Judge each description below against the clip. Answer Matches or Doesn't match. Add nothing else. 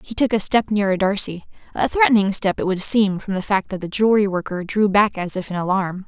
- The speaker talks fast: Matches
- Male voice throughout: Doesn't match